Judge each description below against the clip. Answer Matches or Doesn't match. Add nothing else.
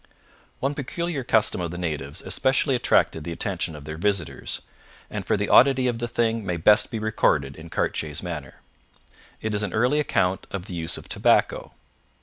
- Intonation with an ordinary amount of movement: Doesn't match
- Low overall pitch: Matches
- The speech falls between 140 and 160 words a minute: Doesn't match